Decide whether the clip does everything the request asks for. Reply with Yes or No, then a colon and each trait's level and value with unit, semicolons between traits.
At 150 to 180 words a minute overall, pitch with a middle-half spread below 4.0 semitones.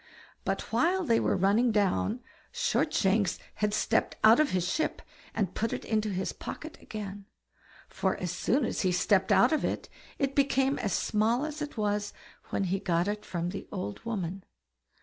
No: average, 175 wpm; average, 4.3 semitones